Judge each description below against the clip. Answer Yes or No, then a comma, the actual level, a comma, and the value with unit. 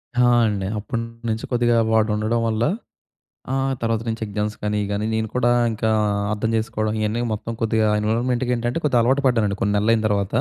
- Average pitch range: No, narrow, 2.0 semitones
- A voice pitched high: No, low, 110 Hz